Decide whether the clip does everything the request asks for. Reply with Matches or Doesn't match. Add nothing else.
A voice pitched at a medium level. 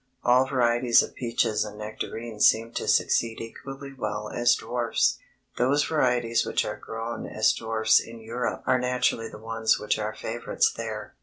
Doesn't match